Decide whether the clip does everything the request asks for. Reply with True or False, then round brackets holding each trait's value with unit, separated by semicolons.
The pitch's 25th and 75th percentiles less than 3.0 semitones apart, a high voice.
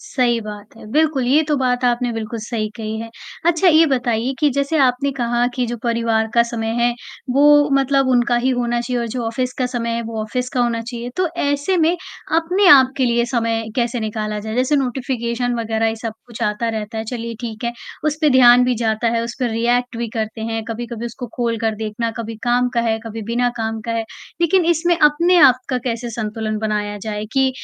True (2.5 semitones; 240 Hz)